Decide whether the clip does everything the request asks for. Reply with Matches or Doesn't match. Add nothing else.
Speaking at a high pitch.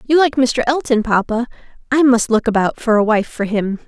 Matches